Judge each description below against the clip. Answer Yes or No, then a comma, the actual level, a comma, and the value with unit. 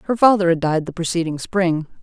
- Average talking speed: No, fast, 210 wpm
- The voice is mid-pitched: Yes, medium, 175 Hz